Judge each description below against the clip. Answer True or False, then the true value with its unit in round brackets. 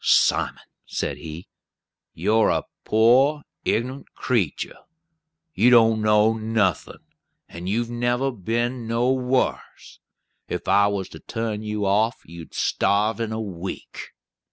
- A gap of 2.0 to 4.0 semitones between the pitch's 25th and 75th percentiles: True (2.8 semitones)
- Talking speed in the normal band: False (120 wpm)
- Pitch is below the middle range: True (110 Hz)